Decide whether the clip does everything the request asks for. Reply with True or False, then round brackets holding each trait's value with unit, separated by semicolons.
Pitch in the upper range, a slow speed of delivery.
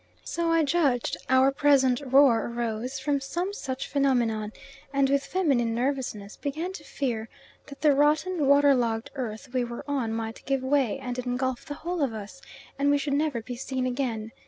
False (270 Hz; 180 wpm)